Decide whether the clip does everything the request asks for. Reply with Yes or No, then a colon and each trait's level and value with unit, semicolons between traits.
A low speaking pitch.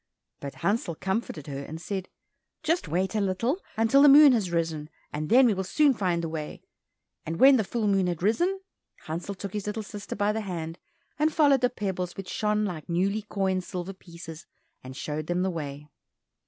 No: high, 190 Hz